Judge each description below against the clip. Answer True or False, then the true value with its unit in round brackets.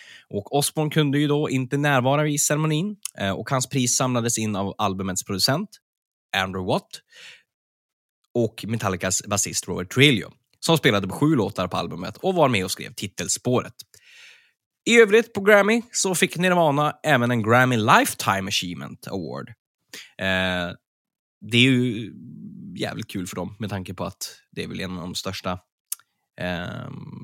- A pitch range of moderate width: False (7.8 semitones)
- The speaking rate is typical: True (155 wpm)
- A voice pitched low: True (125 Hz)